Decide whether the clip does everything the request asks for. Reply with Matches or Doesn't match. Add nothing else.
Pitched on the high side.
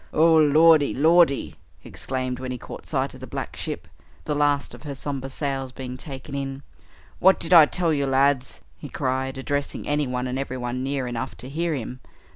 Doesn't match